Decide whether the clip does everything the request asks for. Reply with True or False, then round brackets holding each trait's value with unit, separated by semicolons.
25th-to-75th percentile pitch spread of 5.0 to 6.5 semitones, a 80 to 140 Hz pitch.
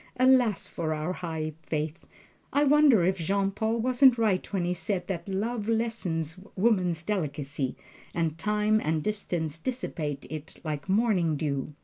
False (5.6 semitones; 185 Hz)